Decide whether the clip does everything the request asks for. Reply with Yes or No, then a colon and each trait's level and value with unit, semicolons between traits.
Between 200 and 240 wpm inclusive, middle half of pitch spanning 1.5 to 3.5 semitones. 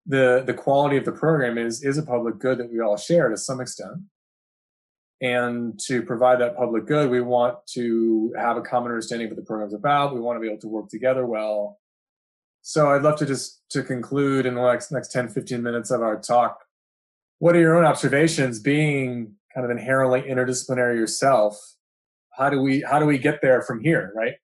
Yes: fast, 205 wpm; average, 3.1 semitones